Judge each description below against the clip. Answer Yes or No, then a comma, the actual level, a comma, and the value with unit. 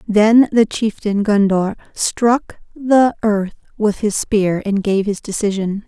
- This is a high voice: Yes, high, 210 Hz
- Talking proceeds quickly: No, average, 145 wpm